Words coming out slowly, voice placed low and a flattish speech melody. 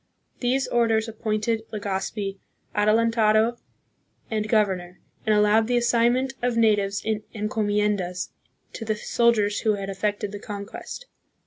No: slow, 120 wpm; high, 215 Hz; narrow, 1.9 semitones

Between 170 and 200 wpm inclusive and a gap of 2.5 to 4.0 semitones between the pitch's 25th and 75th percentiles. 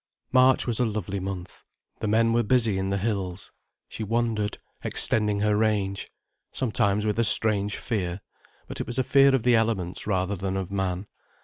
Yes: average, 180 wpm; average, 2.9 semitones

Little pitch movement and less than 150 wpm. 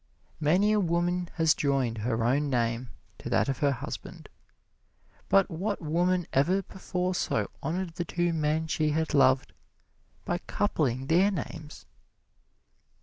No: average, 4.5 semitones; average, 140 wpm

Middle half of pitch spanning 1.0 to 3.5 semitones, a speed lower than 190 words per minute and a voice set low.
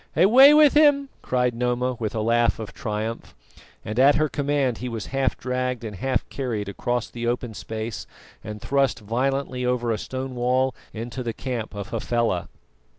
Yes: average, 2.8 semitones; average, 170 wpm; low, 125 Hz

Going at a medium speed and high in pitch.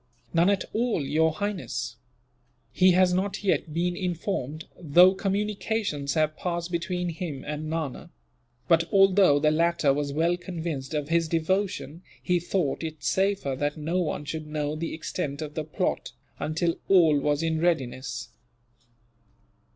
No: average, 145 wpm; medium, 165 Hz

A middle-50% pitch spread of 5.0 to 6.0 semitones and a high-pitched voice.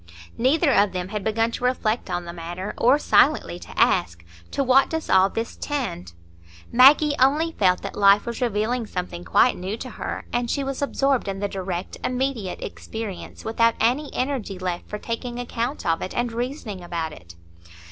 Yes: wide, 5.5 semitones; high, 225 Hz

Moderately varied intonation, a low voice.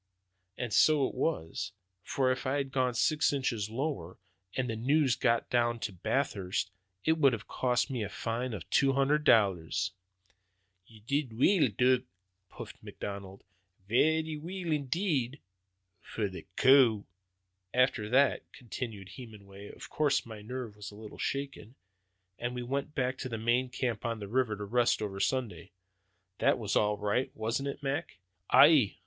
Yes: average, 4.4 semitones; low, 125 Hz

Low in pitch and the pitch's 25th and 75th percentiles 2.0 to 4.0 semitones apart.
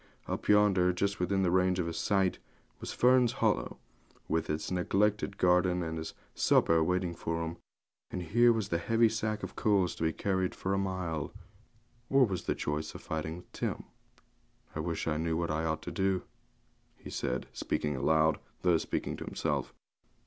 Yes: very low, 90 Hz; average, 3.2 semitones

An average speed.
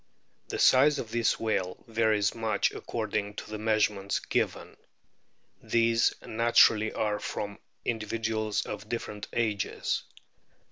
No: slow, 120 wpm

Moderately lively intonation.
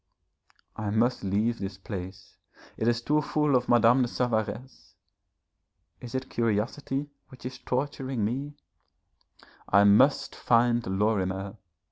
Yes: average, 4.2 semitones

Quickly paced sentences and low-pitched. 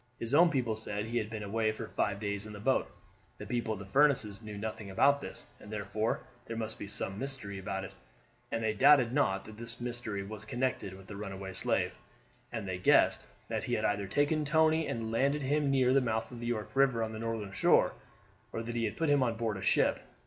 Yes: fast, 230 wpm; low, 110 Hz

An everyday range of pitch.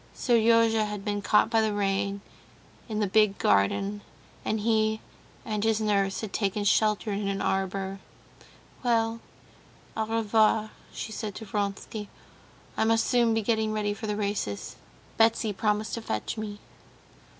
No: narrow, 1.6 semitones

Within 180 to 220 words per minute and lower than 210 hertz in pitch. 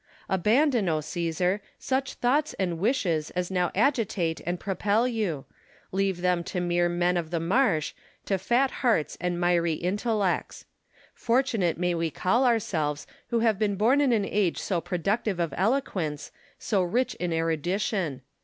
No: average, 155 wpm; medium, 185 Hz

